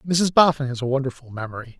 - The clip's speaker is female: No, male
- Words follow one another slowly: No, average, 200 wpm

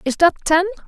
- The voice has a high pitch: Yes, very high, 340 Hz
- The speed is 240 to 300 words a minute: No, fast, 205 wpm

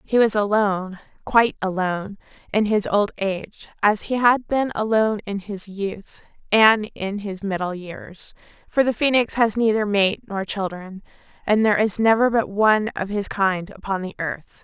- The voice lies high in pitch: Yes, high, 205 Hz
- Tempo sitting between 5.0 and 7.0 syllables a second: No, 4.7 syllables/s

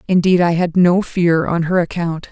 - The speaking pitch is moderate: Yes, medium, 175 Hz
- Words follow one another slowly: No, fast, 205 wpm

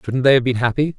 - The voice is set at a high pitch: No, low, 130 Hz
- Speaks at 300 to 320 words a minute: Yes, fast, 305 wpm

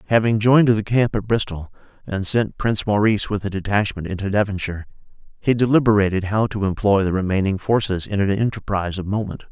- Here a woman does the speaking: No, male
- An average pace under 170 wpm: No, average, 175 wpm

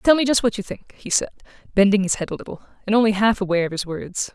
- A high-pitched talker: Yes, high, 205 Hz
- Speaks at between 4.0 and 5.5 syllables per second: No, 6.9 syllables/s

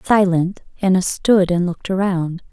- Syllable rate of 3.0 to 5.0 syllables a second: Yes, 4.7 syllables/s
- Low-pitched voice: No, medium, 185 Hz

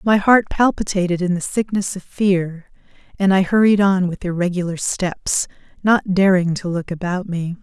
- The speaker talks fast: No, average, 165 wpm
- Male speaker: No, female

